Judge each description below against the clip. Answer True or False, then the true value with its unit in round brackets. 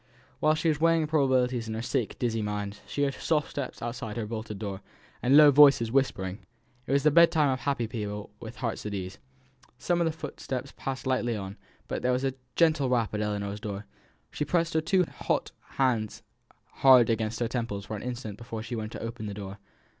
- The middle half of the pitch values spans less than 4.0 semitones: False (4.6 semitones)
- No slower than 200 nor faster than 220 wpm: True (205 wpm)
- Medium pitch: False (120 Hz)